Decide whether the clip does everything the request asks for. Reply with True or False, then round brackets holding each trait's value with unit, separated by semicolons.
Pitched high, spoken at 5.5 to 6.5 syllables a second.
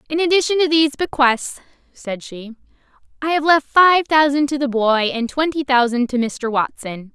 False (275 Hz; 4.8 syllables/s)